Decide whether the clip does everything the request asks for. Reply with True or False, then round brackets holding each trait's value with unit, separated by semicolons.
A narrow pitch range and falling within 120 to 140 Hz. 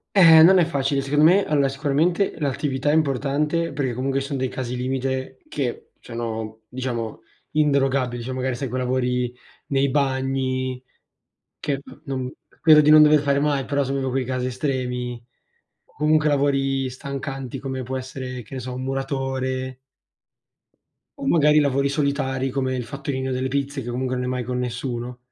True (1.7 semitones; 135 Hz)